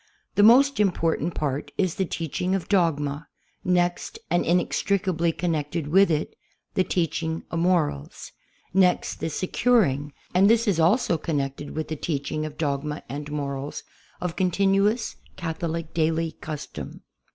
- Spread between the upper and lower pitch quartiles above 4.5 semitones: No, average, 3.5 semitones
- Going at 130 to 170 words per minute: Yes, average, 140 wpm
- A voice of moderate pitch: Yes, medium, 165 Hz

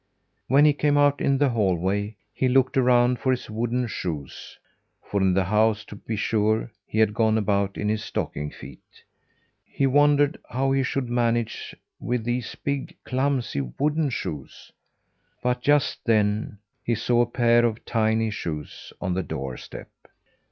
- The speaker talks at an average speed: Yes, average, 160 wpm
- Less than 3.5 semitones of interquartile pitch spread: No, average, 3.9 semitones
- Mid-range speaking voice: No, low, 115 Hz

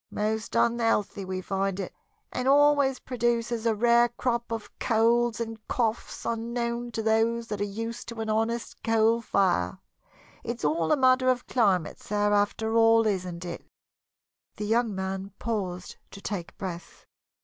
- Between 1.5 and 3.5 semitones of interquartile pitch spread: Yes, average, 2.9 semitones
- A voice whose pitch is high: Yes, high, 225 Hz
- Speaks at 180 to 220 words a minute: No, average, 150 wpm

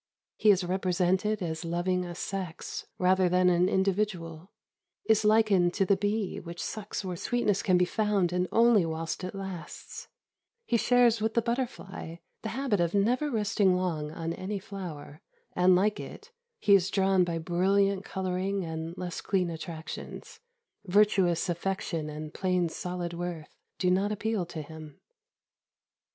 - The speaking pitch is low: No, medium, 185 Hz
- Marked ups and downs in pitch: No, average, 2.9 semitones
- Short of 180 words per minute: Yes, average, 150 wpm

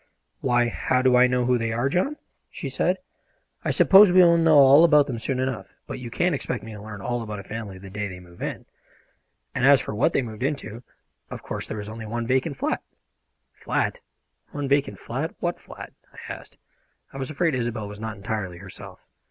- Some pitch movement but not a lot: Yes, average, 4.5 semitones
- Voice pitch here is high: No, low, 120 Hz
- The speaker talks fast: Yes, fast, 210 wpm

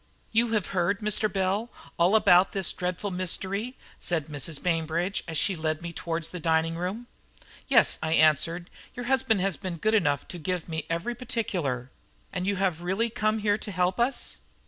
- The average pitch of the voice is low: No, medium, 180 Hz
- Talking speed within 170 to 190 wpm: Yes, average, 180 wpm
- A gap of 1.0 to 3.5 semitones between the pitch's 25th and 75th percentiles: No, average, 4.3 semitones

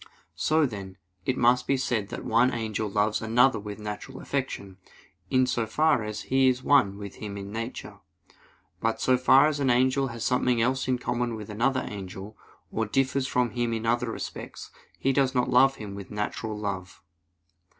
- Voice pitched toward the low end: Yes, low, 120 Hz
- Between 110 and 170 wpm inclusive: No, average, 180 wpm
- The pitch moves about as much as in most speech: Yes, average, 3.6 semitones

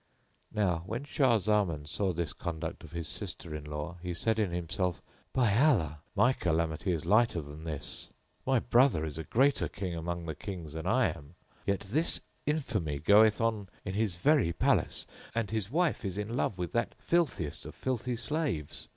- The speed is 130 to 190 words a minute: Yes, average, 180 wpm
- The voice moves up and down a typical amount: No, wide, 6.0 semitones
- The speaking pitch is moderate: No, very low, 95 Hz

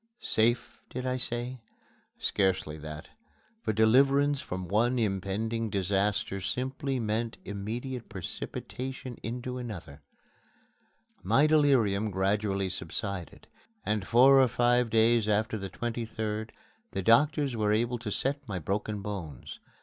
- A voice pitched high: No, low, 110 Hz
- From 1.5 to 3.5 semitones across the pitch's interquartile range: No, average, 4.0 semitones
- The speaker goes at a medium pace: No, slow, 120 wpm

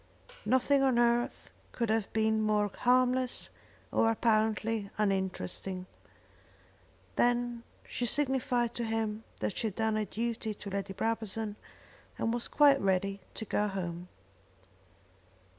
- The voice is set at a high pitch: Yes, high, 220 Hz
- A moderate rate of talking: No, slow, 125 wpm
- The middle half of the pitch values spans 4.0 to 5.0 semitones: No, average, 2.7 semitones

